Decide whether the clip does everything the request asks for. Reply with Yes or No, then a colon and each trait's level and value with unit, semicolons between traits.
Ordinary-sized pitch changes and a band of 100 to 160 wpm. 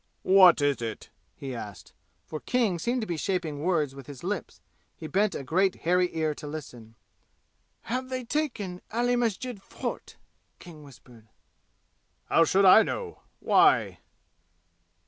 No: wide, 6.9 semitones; average, 145 wpm